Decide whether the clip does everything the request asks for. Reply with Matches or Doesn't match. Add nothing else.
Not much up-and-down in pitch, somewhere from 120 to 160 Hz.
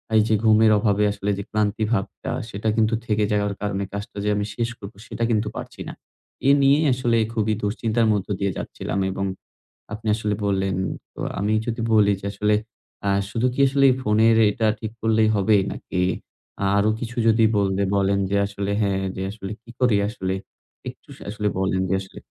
Doesn't match